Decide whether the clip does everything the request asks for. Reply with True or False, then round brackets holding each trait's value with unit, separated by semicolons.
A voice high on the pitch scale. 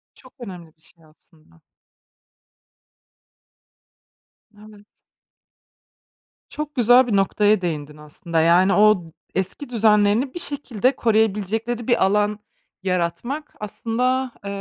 True (210 Hz)